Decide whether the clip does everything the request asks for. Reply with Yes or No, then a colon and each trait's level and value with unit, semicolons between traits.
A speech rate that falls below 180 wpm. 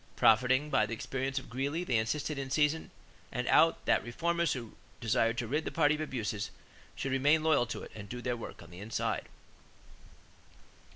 No: average, 185 wpm